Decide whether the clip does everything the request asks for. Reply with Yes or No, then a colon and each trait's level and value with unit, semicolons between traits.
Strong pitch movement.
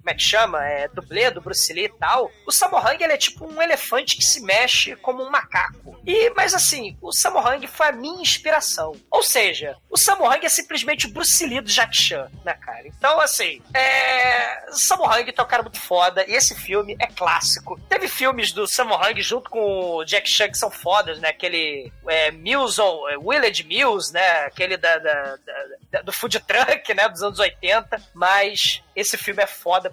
Yes: wide, 8.2 semitones